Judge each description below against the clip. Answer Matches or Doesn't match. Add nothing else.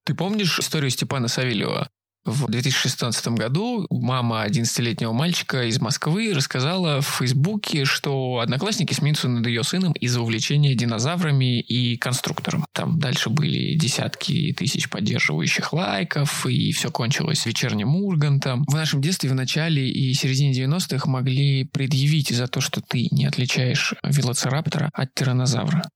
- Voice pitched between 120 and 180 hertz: Matches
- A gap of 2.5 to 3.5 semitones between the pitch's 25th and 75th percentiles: Doesn't match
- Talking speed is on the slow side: Doesn't match